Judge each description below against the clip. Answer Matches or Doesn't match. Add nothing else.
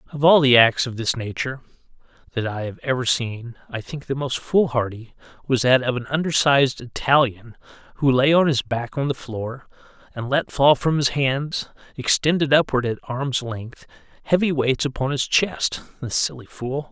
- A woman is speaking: Doesn't match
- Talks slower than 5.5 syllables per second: Matches